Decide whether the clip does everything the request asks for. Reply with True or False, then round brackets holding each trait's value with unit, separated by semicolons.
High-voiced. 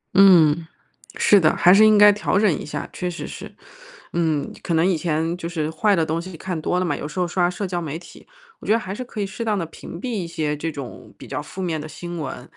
False (175 Hz)